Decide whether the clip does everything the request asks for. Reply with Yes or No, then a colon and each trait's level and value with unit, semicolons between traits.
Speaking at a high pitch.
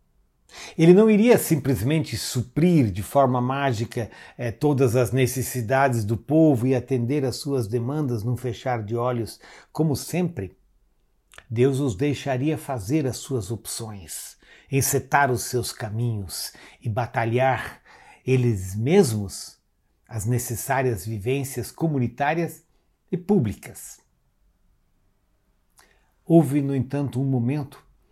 No: low, 130 Hz